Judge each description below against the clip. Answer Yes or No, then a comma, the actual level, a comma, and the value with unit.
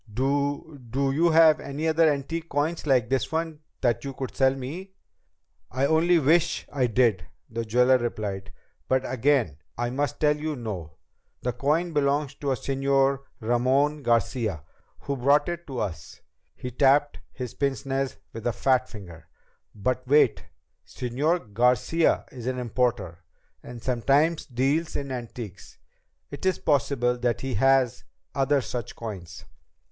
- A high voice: No, low, 135 Hz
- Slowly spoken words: No, average, 150 wpm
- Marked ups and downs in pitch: No, average, 3.3 semitones